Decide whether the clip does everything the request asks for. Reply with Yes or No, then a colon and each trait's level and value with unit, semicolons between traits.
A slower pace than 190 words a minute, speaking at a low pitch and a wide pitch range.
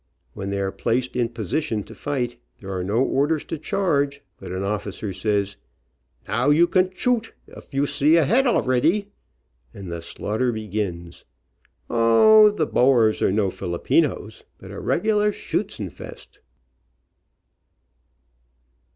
Yes: slow, 135 wpm; low, 125 Hz; wide, 7.8 semitones